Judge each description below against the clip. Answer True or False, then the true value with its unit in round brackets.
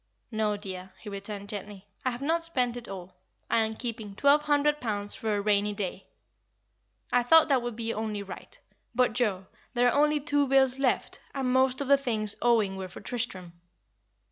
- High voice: True (230 Hz)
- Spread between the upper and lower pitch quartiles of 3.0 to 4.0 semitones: False (4.4 semitones)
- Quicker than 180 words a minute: True (190 wpm)